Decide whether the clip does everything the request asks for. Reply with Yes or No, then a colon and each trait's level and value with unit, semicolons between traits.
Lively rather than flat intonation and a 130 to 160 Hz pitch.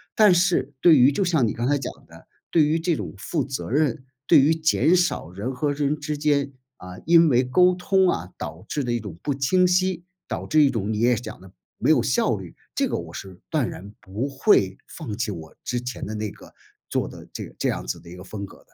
Yes: wide, 7.1 semitones; low, 135 Hz